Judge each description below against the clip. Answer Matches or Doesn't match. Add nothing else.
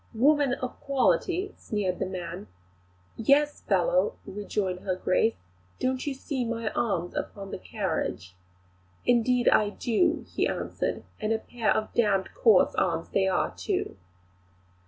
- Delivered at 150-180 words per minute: Doesn't match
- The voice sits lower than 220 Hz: Doesn't match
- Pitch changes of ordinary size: Doesn't match